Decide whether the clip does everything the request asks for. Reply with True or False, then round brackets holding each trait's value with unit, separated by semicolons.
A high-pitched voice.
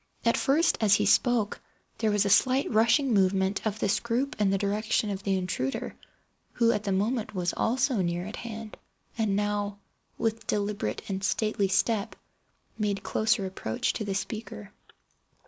True (210 Hz)